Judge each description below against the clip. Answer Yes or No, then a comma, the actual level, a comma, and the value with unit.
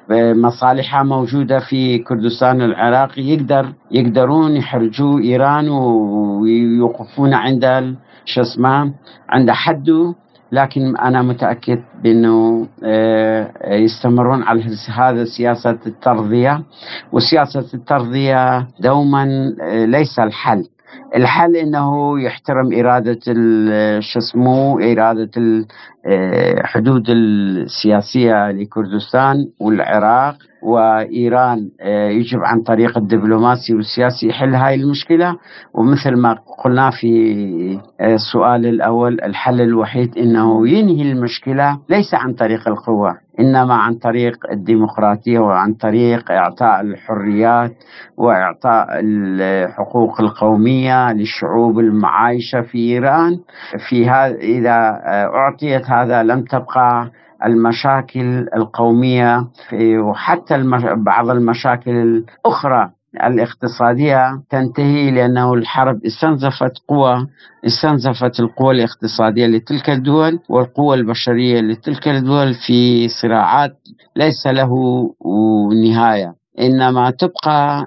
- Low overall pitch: Yes, low, 120 Hz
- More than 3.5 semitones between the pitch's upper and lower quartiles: No, average, 2.8 semitones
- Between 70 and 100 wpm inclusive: Yes, average, 90 wpm